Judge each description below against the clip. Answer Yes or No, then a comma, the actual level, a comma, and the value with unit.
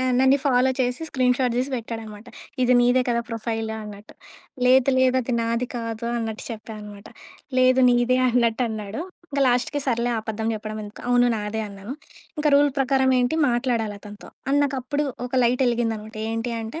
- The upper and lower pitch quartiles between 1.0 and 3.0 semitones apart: Yes, narrow, 2.5 semitones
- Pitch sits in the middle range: No, high, 240 Hz